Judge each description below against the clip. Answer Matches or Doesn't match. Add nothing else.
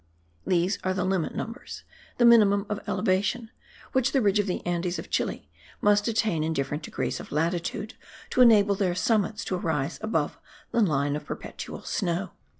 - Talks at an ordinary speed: Matches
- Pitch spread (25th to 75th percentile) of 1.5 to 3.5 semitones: Doesn't match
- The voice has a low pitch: Doesn't match